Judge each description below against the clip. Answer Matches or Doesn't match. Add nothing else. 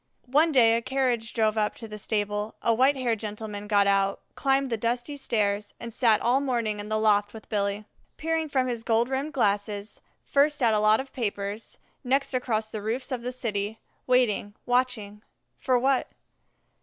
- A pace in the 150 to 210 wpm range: Matches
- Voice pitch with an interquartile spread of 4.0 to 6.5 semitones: Doesn't match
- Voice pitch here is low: Doesn't match